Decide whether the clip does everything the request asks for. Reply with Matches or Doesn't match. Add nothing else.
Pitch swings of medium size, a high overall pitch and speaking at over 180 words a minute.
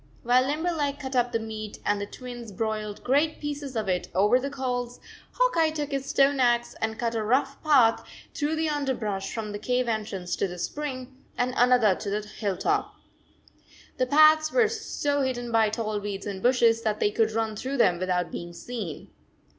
Matches